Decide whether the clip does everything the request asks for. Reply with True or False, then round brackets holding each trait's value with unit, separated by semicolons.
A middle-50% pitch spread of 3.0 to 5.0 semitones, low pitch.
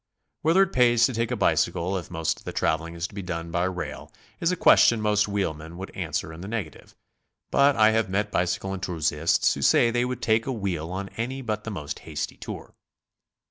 False (5.5 semitones; 100 Hz)